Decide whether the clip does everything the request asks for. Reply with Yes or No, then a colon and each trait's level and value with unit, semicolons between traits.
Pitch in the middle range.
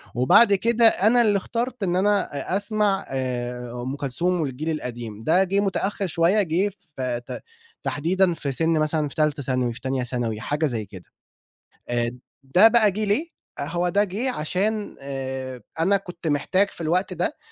Yes: medium, 165 Hz